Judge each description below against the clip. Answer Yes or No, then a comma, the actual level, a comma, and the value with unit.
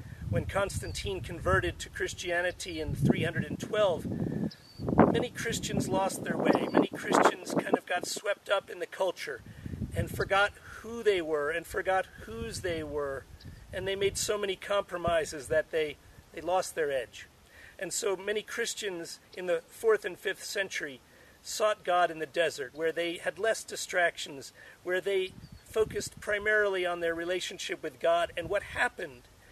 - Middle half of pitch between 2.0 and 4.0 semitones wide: Yes, average, 3.7 semitones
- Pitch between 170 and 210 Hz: Yes, medium, 185 Hz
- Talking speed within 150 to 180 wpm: Yes, average, 155 wpm